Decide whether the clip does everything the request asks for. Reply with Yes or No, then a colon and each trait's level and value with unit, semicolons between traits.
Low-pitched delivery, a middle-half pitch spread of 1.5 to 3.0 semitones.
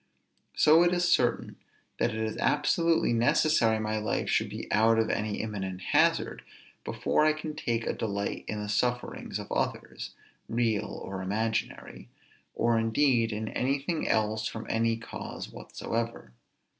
Yes: low, 115 Hz; average, 2.7 semitones